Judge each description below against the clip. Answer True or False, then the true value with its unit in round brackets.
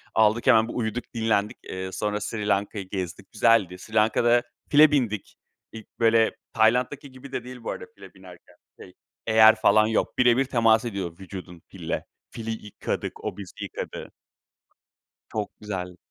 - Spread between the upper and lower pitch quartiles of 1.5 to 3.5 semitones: True (2.8 semitones)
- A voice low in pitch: True (110 Hz)